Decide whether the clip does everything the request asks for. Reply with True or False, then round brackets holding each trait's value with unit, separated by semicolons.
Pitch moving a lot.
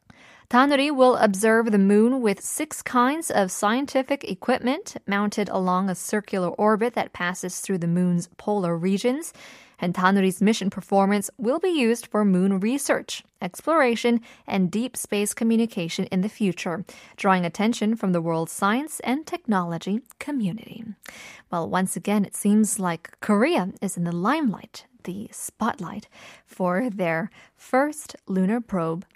False (4.5 semitones)